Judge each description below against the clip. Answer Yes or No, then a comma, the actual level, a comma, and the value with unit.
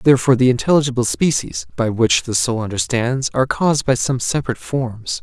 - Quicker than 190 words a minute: No, average, 170 wpm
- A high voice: No, low, 125 Hz